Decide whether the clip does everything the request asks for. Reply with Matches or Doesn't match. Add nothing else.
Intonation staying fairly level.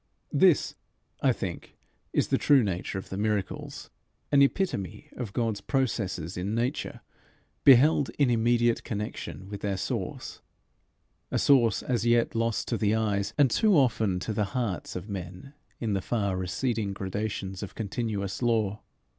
Doesn't match